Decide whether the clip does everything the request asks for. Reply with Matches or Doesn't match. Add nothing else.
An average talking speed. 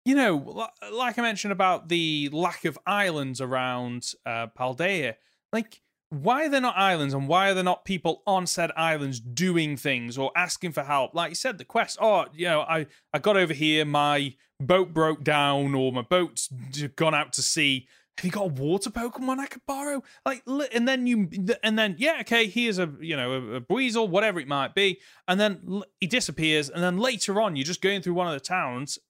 Doesn't match